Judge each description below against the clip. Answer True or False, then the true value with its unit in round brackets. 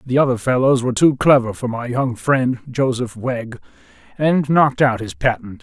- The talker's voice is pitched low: True (125 Hz)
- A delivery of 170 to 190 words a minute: True (180 wpm)